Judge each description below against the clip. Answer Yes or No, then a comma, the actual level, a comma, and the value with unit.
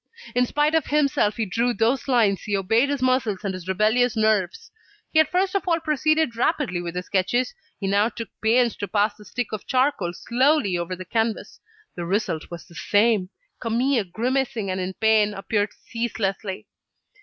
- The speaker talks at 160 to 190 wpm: Yes, average, 180 wpm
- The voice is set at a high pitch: Yes, high, 225 Hz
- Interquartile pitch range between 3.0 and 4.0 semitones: No, average, 4.6 semitones